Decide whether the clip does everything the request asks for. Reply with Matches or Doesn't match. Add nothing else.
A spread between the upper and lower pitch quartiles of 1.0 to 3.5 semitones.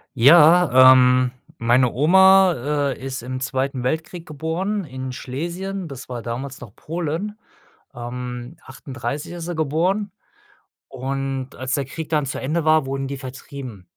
Doesn't match